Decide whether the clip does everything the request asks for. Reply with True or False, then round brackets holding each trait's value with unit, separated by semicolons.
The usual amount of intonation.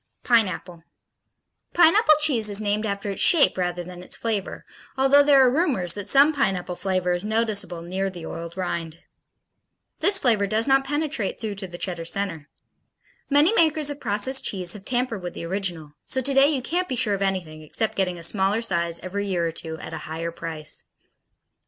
False (6.8 semitones)